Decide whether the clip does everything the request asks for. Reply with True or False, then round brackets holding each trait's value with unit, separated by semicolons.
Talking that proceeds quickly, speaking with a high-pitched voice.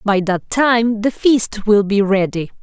False (185 wpm; 210 Hz)